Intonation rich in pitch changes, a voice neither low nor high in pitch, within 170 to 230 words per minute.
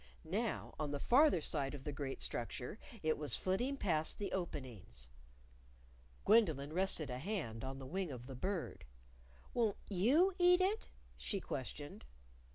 No: wide, 7.6 semitones; medium, 160 Hz; average, 150 wpm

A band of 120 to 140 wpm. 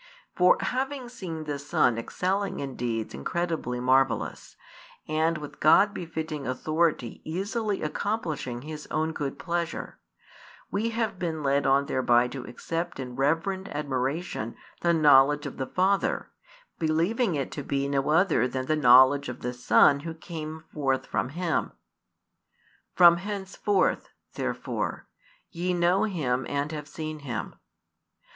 Yes: slow, 135 wpm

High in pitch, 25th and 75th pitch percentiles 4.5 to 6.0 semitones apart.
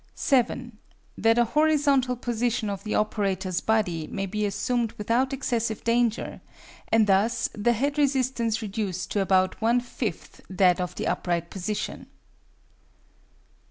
No: high, 220 Hz; average, 3.6 semitones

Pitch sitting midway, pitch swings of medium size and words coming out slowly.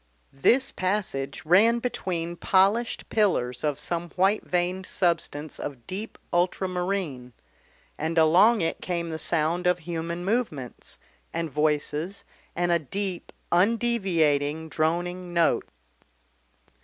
Yes: medium, 175 Hz; average, 3.3 semitones; slow, 110 wpm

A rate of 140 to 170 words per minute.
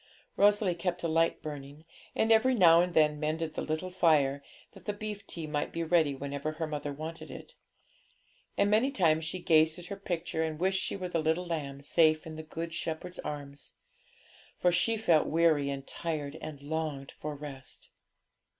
No: average, 185 wpm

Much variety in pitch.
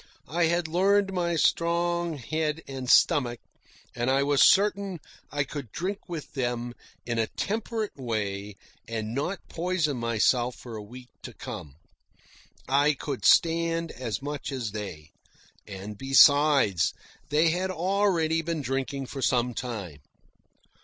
Yes: wide, 5.9 semitones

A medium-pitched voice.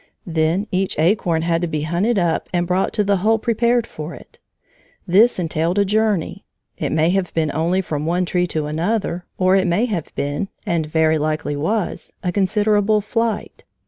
Yes: medium, 180 Hz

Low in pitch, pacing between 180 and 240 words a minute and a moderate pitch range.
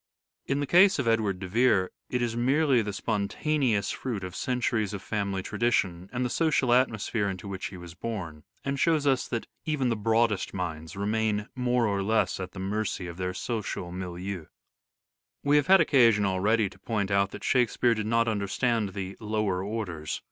Yes: low, 110 Hz; average, 185 wpm; average, 4.1 semitones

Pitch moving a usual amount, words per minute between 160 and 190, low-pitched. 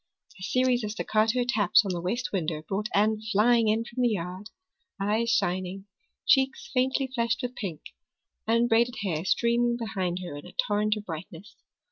No: average, 4.2 semitones; average, 165 wpm; high, 215 Hz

